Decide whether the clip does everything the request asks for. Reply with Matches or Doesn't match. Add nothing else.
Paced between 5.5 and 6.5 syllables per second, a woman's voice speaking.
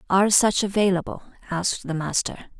Matches